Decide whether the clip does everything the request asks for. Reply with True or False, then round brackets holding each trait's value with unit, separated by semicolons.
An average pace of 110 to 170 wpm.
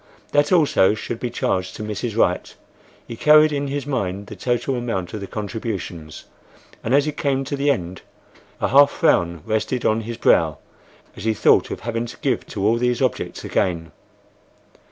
False (180 wpm)